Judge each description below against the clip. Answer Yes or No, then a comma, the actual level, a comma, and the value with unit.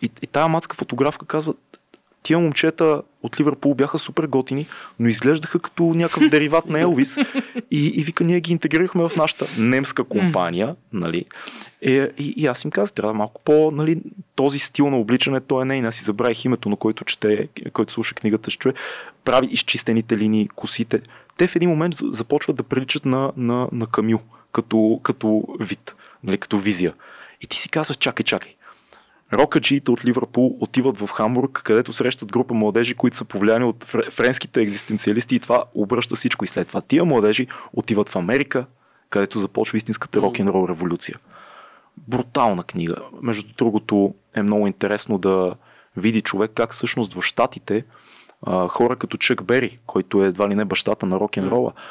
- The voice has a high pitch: No, low, 120 Hz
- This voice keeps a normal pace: No, fast, 170 wpm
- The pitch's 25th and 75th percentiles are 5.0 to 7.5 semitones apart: Yes, average, 5.3 semitones